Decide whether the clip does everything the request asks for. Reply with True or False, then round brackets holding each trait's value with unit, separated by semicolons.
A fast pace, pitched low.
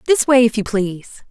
False (230 wpm; 225 Hz)